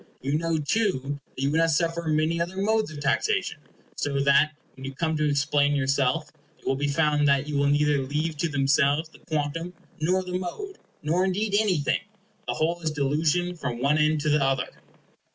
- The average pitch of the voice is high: No, medium, 150 Hz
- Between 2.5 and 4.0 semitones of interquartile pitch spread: Yes, average, 2.9 semitones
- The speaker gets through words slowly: No, average, 195 wpm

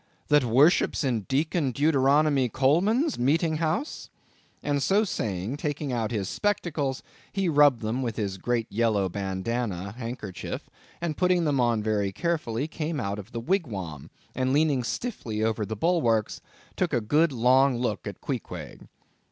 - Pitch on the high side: No, low, 130 Hz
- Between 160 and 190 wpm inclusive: No, average, 150 wpm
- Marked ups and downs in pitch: Yes, wide, 5.9 semitones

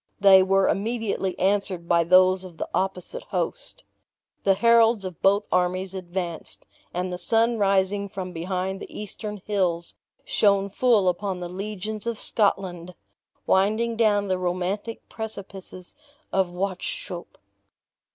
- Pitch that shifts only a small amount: Yes, narrow, 2.2 semitones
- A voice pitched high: Yes, high, 195 Hz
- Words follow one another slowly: Yes, slow, 130 wpm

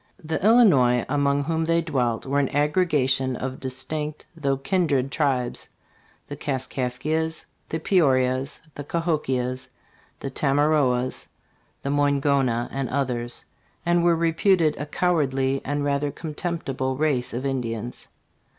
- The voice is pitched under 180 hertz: Yes, medium, 140 Hz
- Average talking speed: No, slow, 125 wpm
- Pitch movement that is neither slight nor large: Yes, average, 3.3 semitones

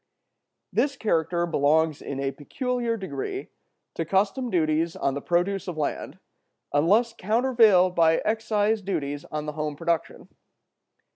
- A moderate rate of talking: No, slow, 130 wpm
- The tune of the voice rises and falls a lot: Yes, wide, 5.9 semitones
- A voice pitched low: No, medium, 175 Hz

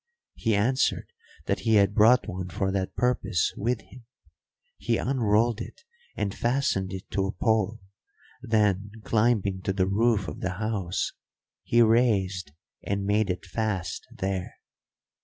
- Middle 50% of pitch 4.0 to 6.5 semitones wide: No, average, 3.1 semitones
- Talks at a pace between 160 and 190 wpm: No, average, 140 wpm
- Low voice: Yes, low, 105 Hz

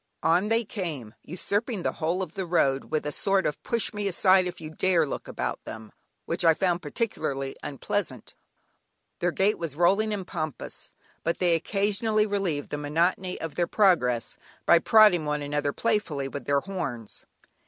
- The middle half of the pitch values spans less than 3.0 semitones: No, average, 4.9 semitones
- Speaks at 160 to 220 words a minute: Yes, average, 170 wpm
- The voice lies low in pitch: No, medium, 175 Hz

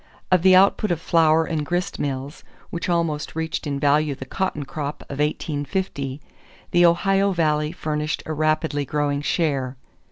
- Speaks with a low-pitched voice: No, medium, 155 Hz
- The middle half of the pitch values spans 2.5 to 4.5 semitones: Yes, average, 2.9 semitones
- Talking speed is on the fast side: No, average, 155 wpm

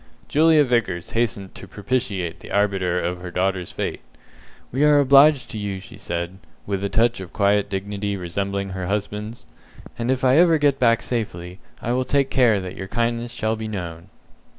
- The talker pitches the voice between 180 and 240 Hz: No, low, 105 Hz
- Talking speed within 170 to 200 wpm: Yes, average, 180 wpm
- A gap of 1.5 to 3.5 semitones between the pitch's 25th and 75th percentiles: No, average, 4.4 semitones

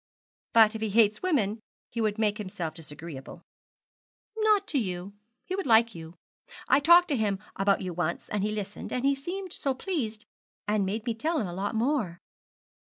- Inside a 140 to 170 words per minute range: No, average, 180 wpm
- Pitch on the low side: No, high, 220 Hz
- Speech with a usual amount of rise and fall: No, wide, 6.0 semitones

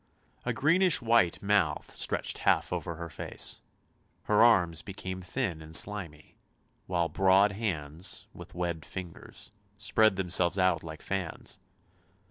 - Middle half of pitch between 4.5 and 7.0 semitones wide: No, average, 3.7 semitones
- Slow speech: Yes, slow, 125 wpm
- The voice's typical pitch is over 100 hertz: No, very low, 95 Hz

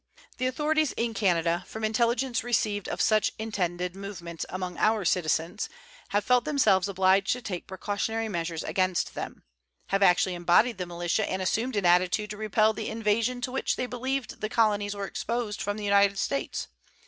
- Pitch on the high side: Yes, high, 205 Hz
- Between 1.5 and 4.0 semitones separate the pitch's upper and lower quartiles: Yes, average, 3.5 semitones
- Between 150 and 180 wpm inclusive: Yes, average, 170 wpm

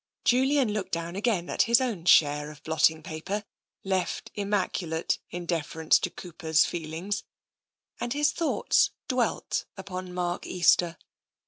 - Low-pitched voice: No, medium, 180 Hz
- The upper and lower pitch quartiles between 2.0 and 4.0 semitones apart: No, average, 4.4 semitones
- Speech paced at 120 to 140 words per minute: Yes, slow, 135 wpm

